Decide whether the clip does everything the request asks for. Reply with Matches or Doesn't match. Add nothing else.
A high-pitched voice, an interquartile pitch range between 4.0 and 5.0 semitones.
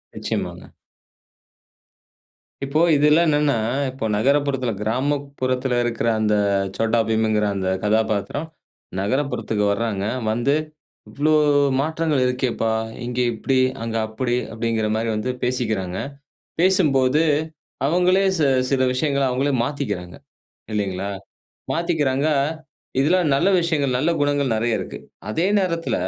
Doesn't match